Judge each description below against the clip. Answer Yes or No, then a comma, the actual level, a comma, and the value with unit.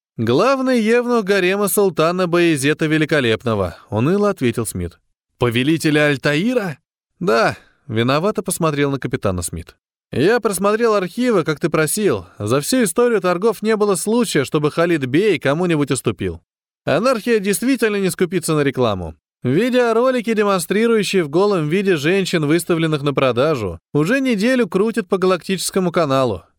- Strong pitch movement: Yes, wide, 7.0 semitones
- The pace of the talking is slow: No, average, 125 wpm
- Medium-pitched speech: Yes, medium, 175 Hz